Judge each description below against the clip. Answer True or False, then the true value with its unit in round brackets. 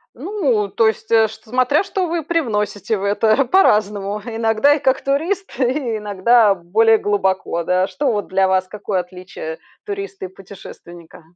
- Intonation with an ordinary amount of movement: True (4.9 semitones)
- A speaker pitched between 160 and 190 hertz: False (215 Hz)